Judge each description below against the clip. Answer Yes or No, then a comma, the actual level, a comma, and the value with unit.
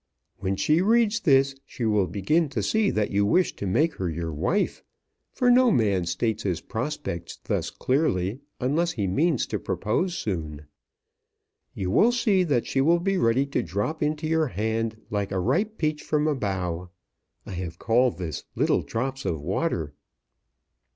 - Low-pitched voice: Yes, low, 120 Hz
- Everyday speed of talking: Yes, average, 170 wpm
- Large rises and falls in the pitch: Yes, wide, 8.9 semitones